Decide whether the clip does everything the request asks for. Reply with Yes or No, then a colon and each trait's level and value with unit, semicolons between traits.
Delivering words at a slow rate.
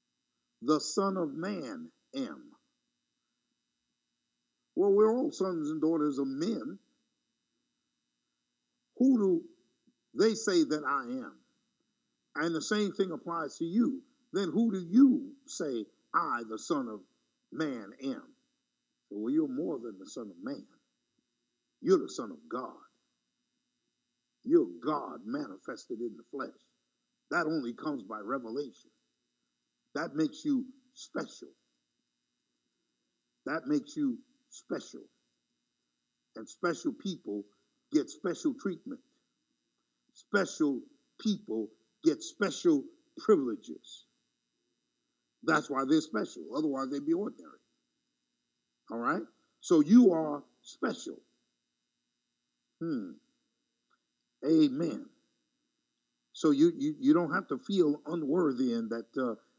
Yes: slow, 110 wpm